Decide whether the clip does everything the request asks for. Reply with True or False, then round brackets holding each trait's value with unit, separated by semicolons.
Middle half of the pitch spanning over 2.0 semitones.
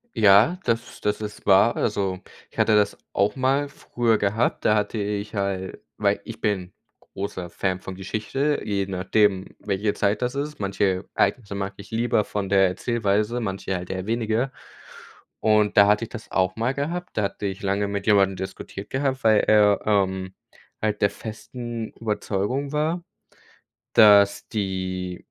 True (2.8 semitones)